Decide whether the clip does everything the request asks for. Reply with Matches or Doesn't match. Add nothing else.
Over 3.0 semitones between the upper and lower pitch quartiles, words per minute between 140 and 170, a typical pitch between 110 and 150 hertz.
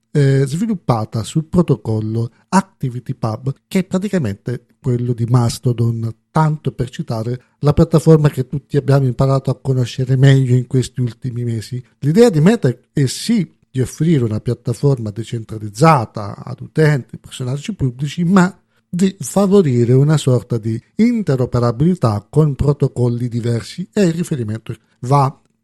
Doesn't match